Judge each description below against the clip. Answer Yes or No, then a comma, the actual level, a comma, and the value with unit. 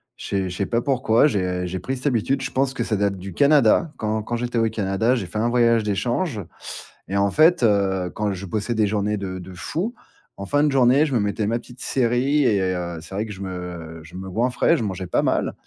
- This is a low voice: Yes, low, 105 Hz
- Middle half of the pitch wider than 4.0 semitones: Yes, average, 4.5 semitones